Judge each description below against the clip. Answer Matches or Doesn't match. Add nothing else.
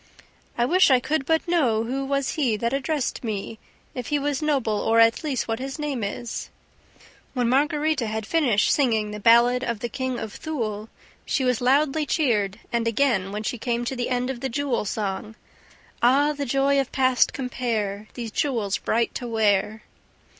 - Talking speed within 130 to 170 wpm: Doesn't match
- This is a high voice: Matches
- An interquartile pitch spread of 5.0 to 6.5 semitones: Doesn't match